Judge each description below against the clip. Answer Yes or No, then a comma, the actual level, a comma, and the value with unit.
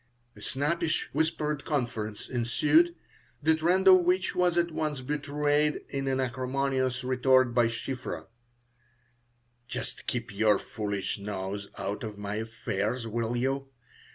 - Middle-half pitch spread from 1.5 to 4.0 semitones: No, average, 5.0 semitones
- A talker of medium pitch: No, low, 130 Hz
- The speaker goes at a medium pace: No, slow, 125 wpm